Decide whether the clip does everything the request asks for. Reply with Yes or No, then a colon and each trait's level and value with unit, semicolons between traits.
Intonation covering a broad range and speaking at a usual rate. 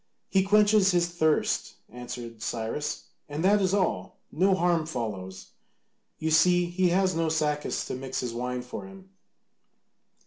Yes: wide, 7.0 semitones; average, 145 wpm